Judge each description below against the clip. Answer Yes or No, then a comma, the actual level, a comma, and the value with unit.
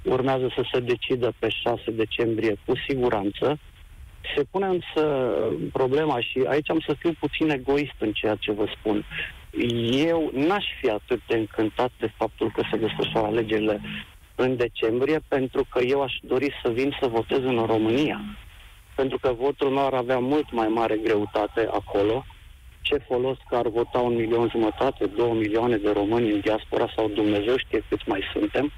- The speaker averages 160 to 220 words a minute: Yes, fast, 170 wpm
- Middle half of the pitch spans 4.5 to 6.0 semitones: No, average, 3.9 semitones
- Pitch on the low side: Yes, low, 120 Hz